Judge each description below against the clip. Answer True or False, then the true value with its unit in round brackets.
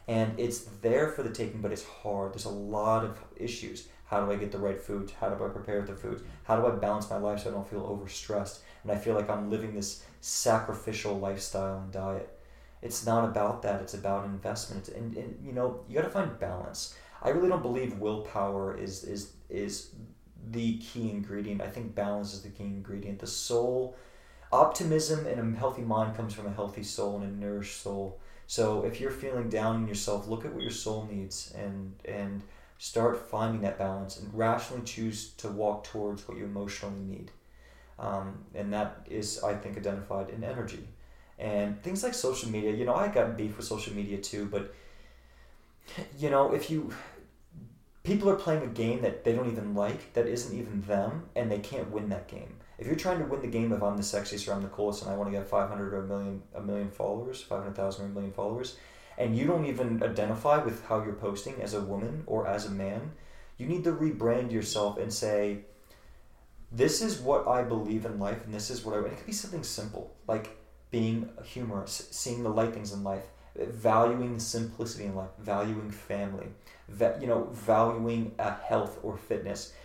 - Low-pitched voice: True (105 Hz)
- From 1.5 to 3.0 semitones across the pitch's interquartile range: True (2.6 semitones)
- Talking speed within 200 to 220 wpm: True (205 wpm)